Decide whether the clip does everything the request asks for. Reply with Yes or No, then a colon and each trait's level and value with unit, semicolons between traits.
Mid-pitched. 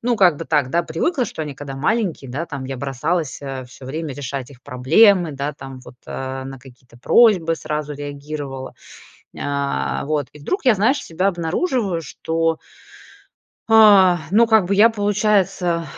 Yes: medium, 155 Hz